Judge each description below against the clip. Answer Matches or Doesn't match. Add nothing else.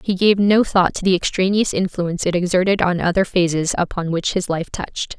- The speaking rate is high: Matches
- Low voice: Doesn't match